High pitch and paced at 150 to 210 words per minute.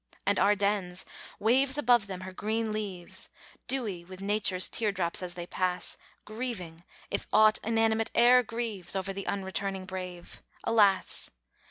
No: high, 200 Hz; average, 140 wpm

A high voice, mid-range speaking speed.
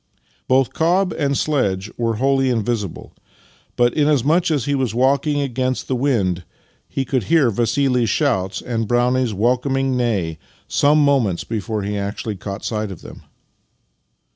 No: low, 125 Hz; average, 145 wpm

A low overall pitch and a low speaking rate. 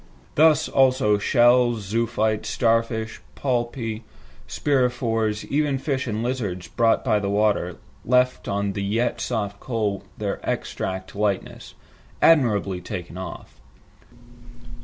Yes: low, 115 Hz; slow, 115 wpm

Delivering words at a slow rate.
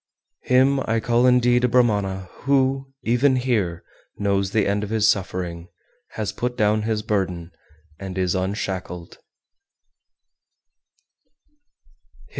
Yes: slow, 115 wpm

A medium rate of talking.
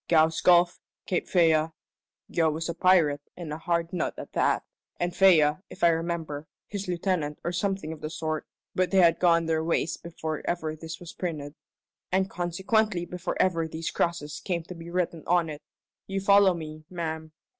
Yes: average, 180 wpm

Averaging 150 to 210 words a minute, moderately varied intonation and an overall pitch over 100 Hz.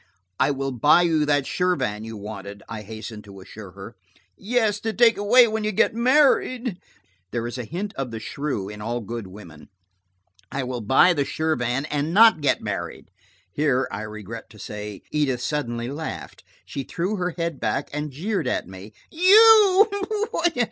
No: average, 170 wpm; wide, 8.9 semitones; medium, 140 Hz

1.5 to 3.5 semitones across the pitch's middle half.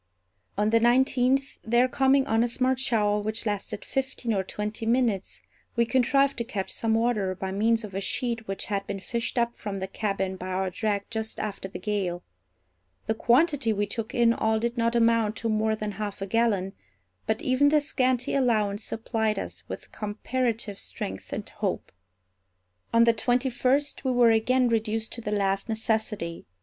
Yes: average, 2.8 semitones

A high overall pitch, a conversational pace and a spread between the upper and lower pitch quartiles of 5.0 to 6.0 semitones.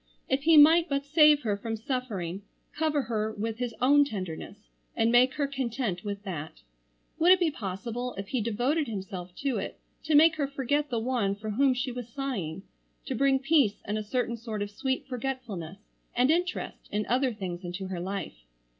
Yes: high, 240 Hz; average, 190 wpm; wide, 5.4 semitones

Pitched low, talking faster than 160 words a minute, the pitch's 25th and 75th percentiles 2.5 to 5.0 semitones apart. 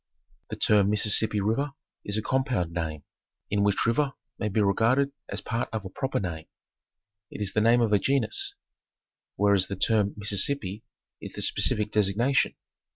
Yes: low, 105 Hz; average, 170 wpm; average, 2.9 semitones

